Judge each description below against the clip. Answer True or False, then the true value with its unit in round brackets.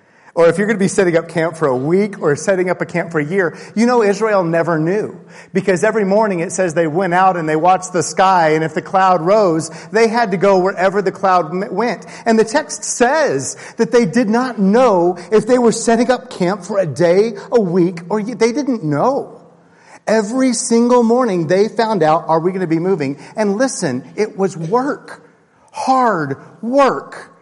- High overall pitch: True (195 Hz)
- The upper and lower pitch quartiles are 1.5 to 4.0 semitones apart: False (4.7 semitones)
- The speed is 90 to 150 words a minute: False (205 wpm)